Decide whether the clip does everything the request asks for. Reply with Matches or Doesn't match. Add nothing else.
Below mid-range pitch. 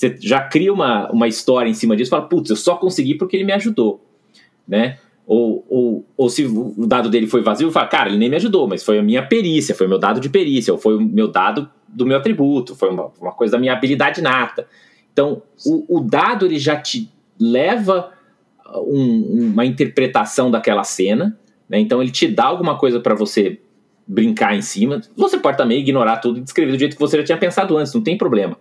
Doesn't match